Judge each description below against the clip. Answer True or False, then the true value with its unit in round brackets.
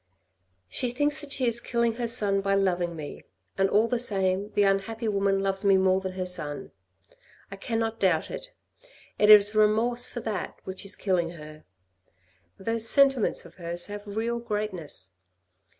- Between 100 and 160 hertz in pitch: False (200 Hz)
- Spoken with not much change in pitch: False (3.5 semitones)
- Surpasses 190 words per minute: False (170 wpm)